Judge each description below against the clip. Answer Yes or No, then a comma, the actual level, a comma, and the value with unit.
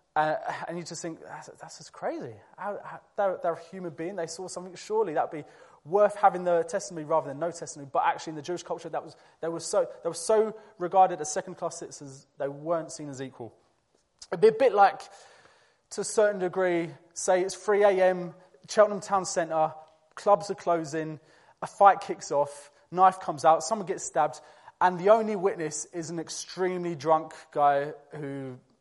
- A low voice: No, medium, 170 Hz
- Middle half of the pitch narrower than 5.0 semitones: Yes, average, 3.3 semitones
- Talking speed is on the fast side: No, average, 190 wpm